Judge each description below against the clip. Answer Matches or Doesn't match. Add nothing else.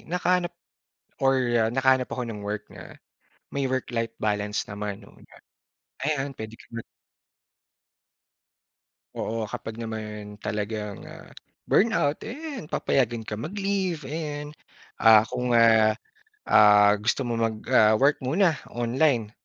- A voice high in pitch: Doesn't match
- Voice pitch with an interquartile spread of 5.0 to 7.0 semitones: Matches